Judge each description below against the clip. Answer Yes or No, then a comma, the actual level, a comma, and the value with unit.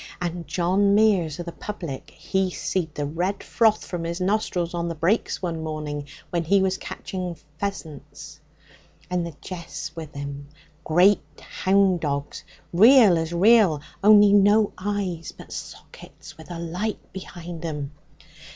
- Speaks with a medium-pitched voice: Yes, medium, 175 Hz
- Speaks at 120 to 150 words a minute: Yes, average, 145 wpm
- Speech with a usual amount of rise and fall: Yes, average, 3.5 semitones